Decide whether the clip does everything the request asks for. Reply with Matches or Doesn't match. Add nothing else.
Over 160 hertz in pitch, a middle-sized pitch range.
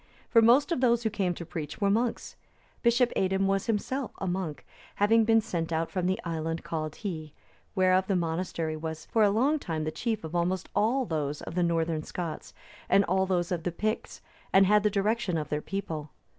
Matches